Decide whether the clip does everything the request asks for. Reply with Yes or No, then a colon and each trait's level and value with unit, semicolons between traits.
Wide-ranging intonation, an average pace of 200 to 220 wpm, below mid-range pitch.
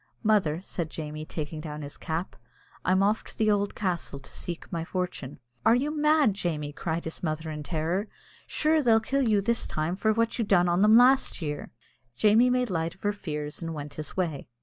No: wide, 5.7 semitones; fast, 205 wpm; medium, 180 Hz